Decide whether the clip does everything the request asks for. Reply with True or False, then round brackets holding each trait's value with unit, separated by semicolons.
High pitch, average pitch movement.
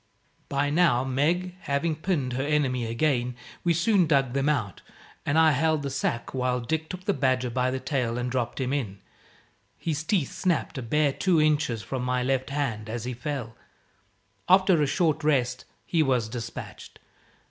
False (135 Hz; 3.9 semitones)